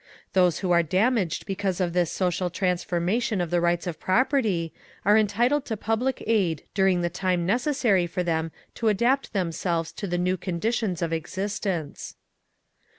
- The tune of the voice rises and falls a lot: No, average, 3.8 semitones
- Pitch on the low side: No, medium, 185 Hz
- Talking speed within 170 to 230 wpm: No, average, 155 wpm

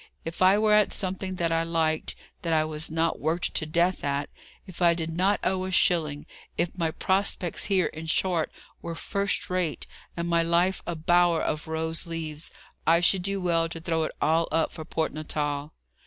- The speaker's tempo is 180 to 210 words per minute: Yes, average, 195 wpm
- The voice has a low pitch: No, medium, 165 Hz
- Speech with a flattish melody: Yes, narrow, 2.3 semitones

